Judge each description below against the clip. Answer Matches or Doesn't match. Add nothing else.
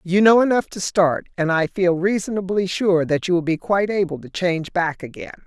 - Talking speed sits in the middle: Doesn't match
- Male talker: Doesn't match